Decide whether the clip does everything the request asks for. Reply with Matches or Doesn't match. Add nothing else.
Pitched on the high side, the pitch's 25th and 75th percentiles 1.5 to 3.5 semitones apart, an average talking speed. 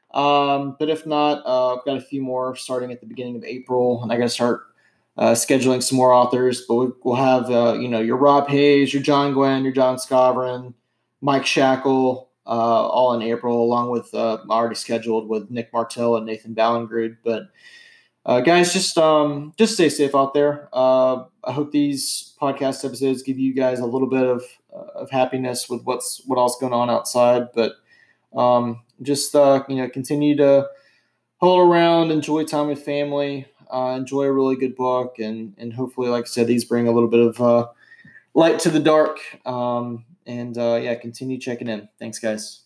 Doesn't match